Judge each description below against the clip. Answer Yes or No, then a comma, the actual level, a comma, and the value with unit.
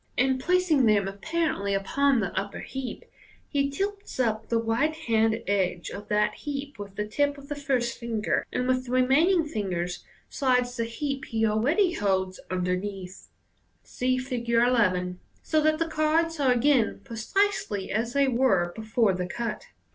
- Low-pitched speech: No, high, 240 Hz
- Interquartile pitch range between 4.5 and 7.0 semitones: Yes, wide, 5.4 semitones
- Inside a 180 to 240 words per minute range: No, average, 160 wpm